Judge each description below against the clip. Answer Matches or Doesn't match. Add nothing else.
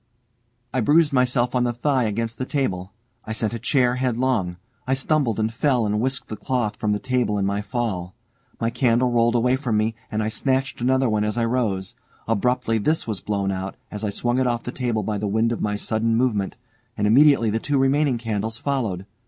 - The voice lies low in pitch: Matches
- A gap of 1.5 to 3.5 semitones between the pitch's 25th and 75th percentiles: Matches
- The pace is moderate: Doesn't match